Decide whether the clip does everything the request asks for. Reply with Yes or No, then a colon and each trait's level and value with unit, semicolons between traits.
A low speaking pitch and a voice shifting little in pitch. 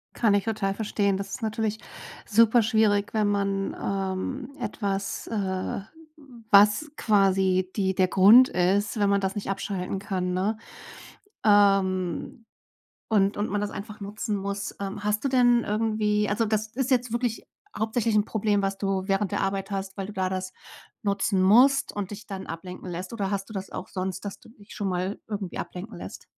No: high, 200 Hz; narrow, 2.0 semitones